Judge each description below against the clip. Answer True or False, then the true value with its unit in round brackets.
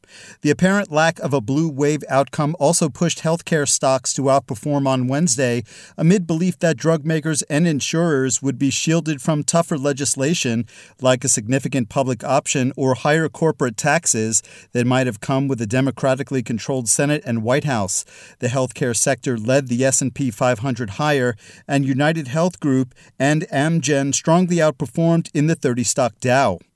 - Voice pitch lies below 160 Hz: True (140 Hz)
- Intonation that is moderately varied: True (3.4 semitones)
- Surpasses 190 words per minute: False (160 wpm)